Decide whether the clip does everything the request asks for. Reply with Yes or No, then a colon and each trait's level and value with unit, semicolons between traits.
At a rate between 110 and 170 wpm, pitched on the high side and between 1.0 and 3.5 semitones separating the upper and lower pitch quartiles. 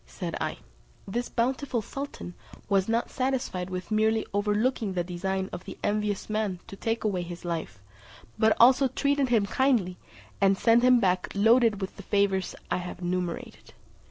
No: average, 160 wpm; high, 205 Hz; average, 4.2 semitones